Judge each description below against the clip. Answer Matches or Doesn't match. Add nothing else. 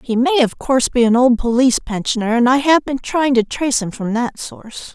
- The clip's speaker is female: Matches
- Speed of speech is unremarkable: Doesn't match